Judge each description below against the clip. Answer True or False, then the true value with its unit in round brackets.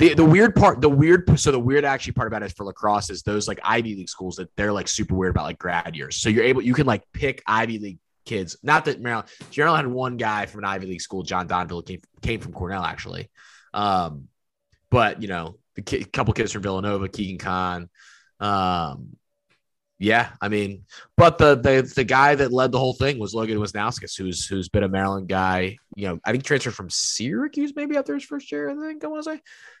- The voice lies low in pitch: True (105 Hz)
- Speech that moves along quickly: True (230 wpm)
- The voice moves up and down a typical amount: False (6.4 semitones)